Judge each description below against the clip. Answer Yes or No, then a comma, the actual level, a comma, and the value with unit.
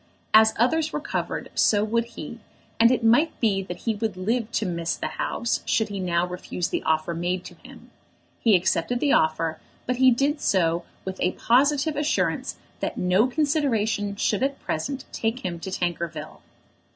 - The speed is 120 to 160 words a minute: No, average, 175 wpm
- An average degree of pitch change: No, wide, 5.8 semitones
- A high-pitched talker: Yes, high, 215 Hz